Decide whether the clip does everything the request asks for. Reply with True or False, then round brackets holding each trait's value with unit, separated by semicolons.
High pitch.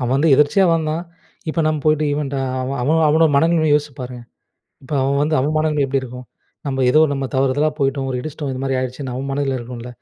False (140 Hz)